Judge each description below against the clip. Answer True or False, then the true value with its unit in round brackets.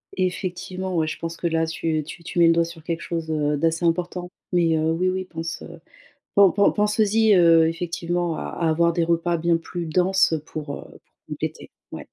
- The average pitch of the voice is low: False (170 Hz)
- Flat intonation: True (1.8 semitones)